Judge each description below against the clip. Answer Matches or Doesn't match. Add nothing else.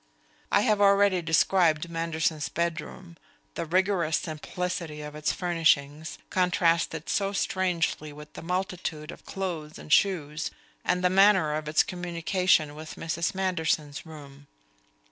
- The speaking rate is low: Matches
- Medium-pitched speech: Matches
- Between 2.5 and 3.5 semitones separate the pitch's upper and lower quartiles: Matches